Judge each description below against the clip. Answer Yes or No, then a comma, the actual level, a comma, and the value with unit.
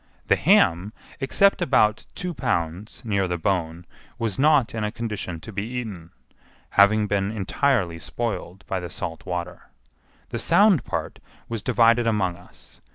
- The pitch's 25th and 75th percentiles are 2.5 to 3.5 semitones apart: No, average, 4.7 semitones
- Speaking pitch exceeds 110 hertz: No, low, 105 Hz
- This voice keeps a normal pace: Yes, average, 150 wpm